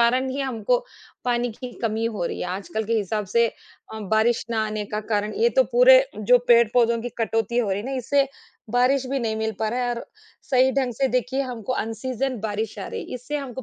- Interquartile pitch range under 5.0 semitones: Yes, average, 2.9 semitones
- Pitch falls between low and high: No, high, 240 Hz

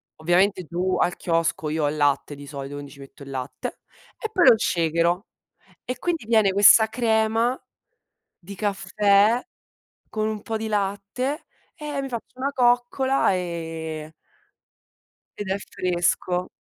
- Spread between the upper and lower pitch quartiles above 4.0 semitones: Yes, wide, 5.4 semitones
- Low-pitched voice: No, high, 200 Hz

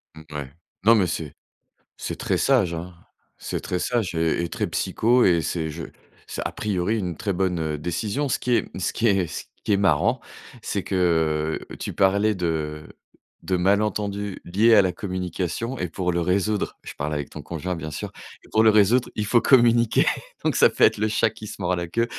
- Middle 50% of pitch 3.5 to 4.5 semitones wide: Yes, average, 4.2 semitones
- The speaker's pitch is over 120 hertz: No, very low, 95 Hz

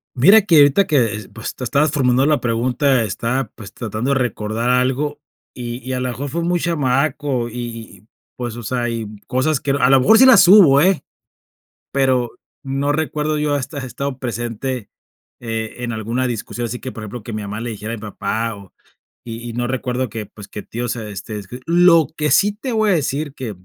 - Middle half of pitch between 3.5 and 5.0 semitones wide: Yes, average, 3.9 semitones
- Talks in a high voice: No, low, 125 Hz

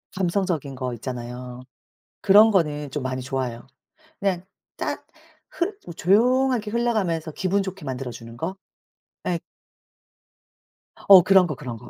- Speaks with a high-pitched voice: No, medium, 170 Hz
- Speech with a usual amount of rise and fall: No, wide, 7.3 semitones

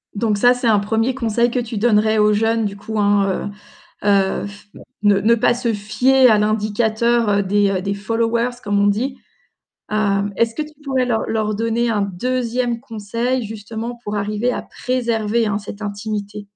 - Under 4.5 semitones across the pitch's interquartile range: Yes, narrow, 2.5 semitones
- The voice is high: Yes, high, 220 Hz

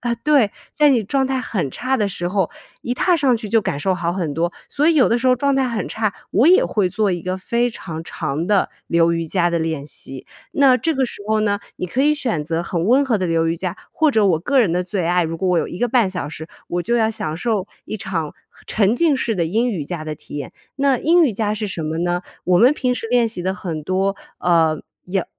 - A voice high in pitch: Yes, high, 195 Hz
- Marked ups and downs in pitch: Yes, wide, 6.3 semitones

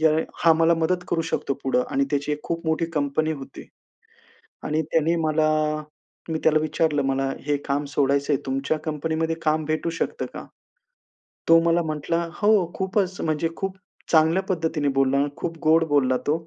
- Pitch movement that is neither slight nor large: No, narrow, 2.3 semitones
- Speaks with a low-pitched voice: No, medium, 155 Hz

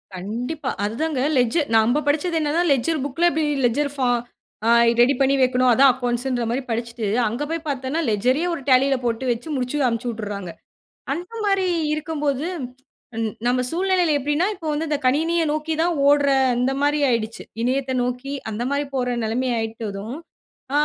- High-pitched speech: Yes, very high, 265 Hz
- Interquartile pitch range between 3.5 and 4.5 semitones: Yes, average, 4.0 semitones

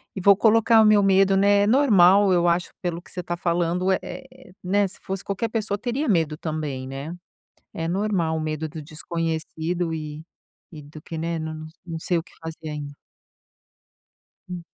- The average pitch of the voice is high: No, medium, 175 Hz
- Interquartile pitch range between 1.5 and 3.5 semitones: No, average, 3.9 semitones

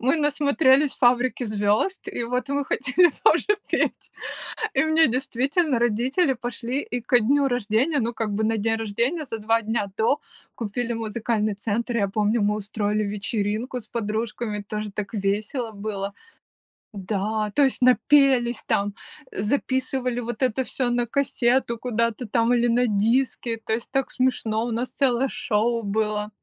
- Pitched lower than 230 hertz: No, high, 235 Hz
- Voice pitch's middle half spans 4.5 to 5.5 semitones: No, average, 3.2 semitones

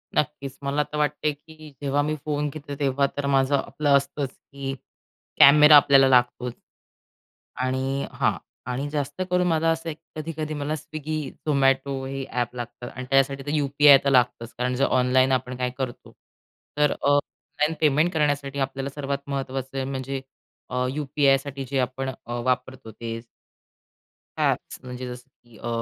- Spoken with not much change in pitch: Yes, narrow, 2.2 semitones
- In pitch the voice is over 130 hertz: Yes, medium, 140 Hz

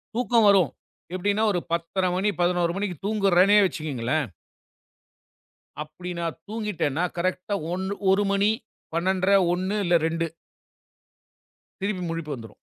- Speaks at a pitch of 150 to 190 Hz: Yes, medium, 185 Hz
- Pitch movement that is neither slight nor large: Yes, average, 3.0 semitones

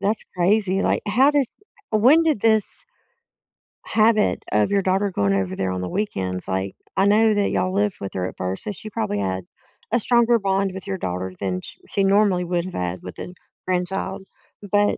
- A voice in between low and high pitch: No, high, 195 Hz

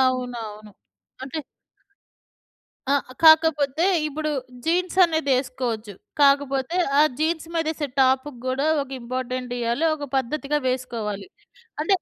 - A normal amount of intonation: Yes, average, 3.8 semitones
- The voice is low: No, very high, 270 Hz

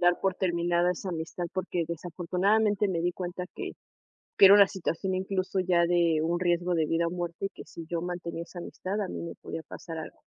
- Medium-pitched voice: Yes, medium, 175 Hz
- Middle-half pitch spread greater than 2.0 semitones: No, narrow, 1.7 semitones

